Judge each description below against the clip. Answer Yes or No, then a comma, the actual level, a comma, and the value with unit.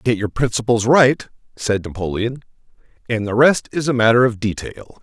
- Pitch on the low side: Yes, low, 120 Hz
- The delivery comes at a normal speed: Yes, average, 165 wpm